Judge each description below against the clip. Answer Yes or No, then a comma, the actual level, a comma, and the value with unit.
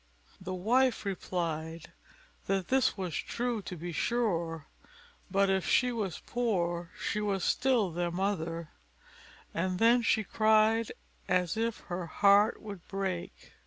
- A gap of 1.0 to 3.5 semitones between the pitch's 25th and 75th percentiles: No, average, 4.2 semitones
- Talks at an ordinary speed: No, slow, 130 wpm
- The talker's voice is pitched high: Yes, high, 195 Hz